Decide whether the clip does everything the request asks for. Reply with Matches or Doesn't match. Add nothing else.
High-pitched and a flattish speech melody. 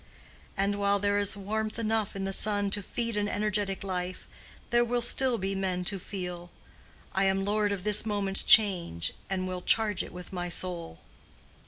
Matches